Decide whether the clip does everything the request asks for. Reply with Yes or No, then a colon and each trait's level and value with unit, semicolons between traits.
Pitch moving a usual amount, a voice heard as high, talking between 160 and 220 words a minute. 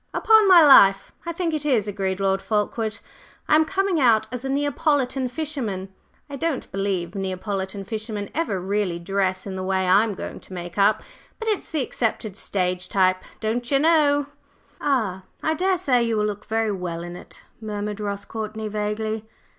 No: wide, 6.2 semitones; high, 215 Hz; average, 170 wpm